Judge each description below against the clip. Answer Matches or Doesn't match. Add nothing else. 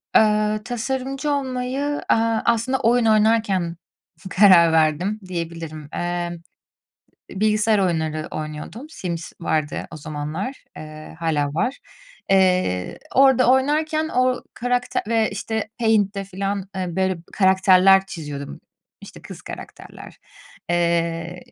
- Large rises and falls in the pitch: Matches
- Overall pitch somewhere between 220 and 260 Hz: Doesn't match